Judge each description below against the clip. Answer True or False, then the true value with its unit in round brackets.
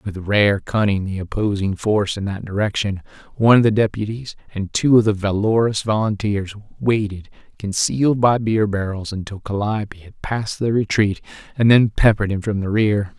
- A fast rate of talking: False (165 wpm)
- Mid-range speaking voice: False (105 Hz)